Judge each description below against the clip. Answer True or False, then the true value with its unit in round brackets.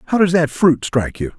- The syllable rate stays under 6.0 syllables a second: False (6.3 syllables/s)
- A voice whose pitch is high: False (145 Hz)